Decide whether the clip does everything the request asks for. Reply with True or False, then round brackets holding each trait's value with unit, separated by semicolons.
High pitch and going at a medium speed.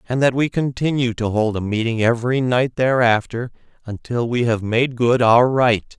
False (120 Hz; 180 wpm)